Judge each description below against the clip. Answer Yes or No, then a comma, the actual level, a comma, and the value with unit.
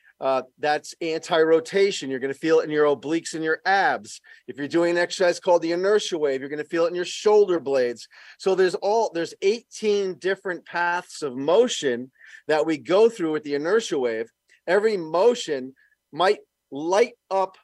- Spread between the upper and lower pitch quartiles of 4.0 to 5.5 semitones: Yes, average, 4.6 semitones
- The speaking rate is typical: Yes, average, 185 wpm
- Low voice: No, medium, 175 Hz